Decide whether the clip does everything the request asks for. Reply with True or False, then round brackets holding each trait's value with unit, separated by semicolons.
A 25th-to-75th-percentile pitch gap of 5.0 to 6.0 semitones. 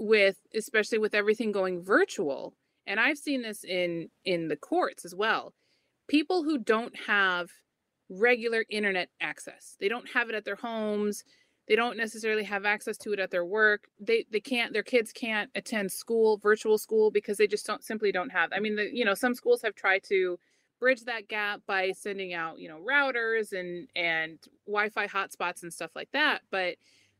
False (3.2 semitones)